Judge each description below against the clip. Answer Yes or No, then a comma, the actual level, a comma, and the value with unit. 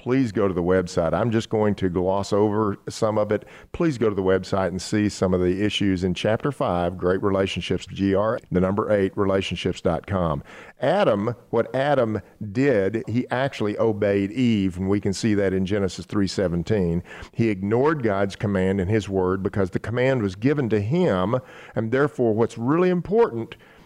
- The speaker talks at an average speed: Yes, average, 175 wpm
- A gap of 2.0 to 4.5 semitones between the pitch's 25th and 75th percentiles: Yes, average, 3.4 semitones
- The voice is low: Yes, low, 105 Hz